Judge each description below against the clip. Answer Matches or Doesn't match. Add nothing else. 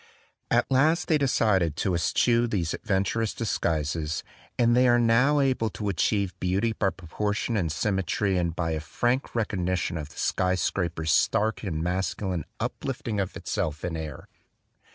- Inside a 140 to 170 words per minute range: Matches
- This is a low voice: Matches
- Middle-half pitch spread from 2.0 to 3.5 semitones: Doesn't match